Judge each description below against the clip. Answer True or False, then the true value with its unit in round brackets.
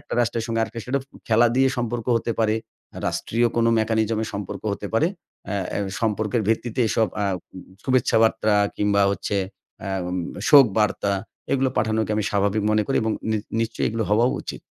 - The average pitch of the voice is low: True (110 Hz)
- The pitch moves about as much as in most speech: False (1.8 semitones)